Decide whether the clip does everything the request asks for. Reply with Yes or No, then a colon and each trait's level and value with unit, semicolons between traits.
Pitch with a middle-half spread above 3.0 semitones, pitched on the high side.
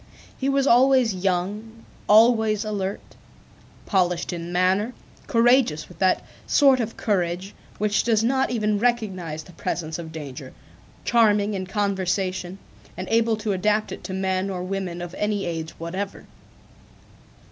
Yes: average, 3.7 semitones; high, 200 Hz